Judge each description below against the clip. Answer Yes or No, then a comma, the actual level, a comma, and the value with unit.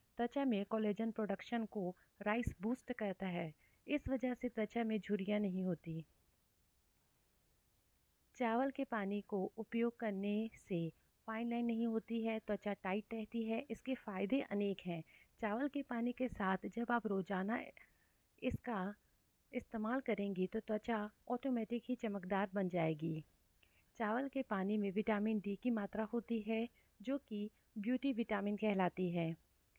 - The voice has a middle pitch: No, high, 215 Hz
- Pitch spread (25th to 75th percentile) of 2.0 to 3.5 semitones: Yes, average, 3.2 semitones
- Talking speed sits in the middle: Yes, average, 145 wpm